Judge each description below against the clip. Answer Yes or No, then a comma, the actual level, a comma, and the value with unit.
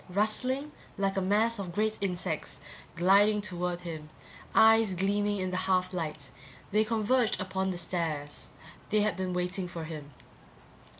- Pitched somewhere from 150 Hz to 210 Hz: Yes, high, 190 Hz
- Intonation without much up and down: No, average, 3.0 semitones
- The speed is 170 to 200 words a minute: No, average, 145 wpm